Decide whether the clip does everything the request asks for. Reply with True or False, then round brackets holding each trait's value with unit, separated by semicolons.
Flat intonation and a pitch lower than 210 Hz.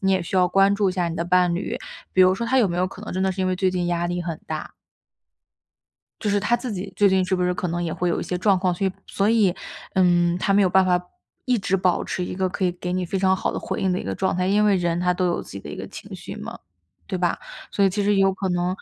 True (1.6 semitones; 185 Hz)